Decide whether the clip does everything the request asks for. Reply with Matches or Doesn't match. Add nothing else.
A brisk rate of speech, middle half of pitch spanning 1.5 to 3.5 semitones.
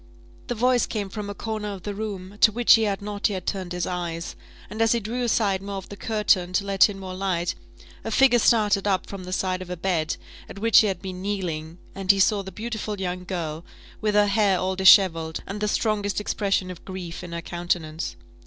Matches